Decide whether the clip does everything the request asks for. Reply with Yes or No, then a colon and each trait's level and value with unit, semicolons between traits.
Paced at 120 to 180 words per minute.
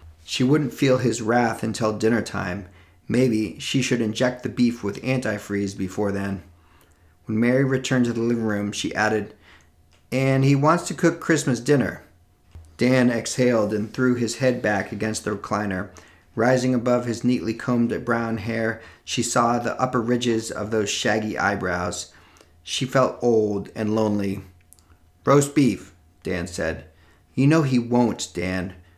Yes: average, 155 wpm